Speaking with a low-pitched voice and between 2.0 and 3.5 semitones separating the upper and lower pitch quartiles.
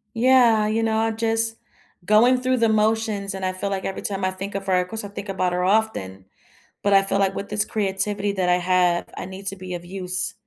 No: high, 200 Hz; average, 2.9 semitones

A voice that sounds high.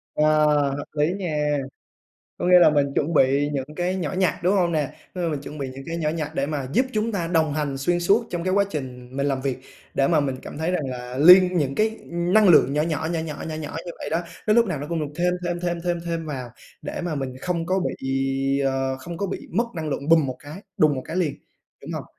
No: medium, 160 Hz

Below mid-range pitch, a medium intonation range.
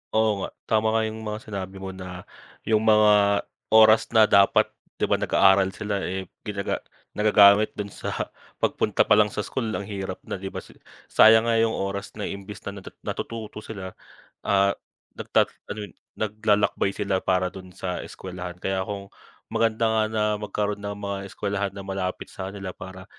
No: low, 100 Hz; narrow, 1.9 semitones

